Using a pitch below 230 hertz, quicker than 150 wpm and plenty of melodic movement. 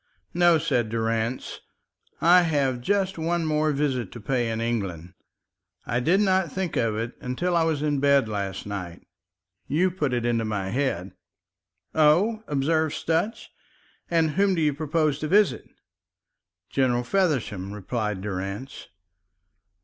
No: medium, 140 Hz; average, 140 wpm; wide, 6.4 semitones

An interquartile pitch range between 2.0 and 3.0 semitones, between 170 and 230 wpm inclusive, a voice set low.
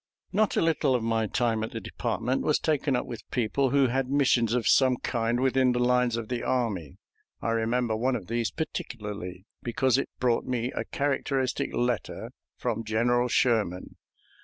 Yes: narrow, 2.5 semitones; average, 175 wpm; low, 120 Hz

